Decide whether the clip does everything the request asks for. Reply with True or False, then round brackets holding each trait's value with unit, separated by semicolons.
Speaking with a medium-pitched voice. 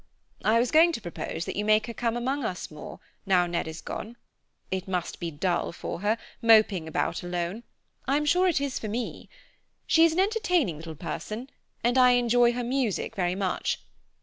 False (225 Hz)